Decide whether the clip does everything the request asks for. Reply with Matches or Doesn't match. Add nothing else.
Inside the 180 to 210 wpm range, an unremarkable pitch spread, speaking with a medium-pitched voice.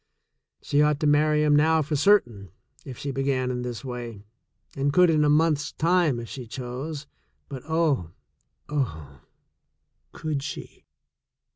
Doesn't match